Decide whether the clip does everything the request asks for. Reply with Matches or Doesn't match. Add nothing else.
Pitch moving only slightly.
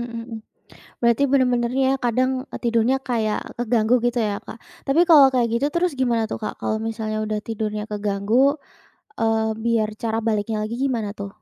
Matches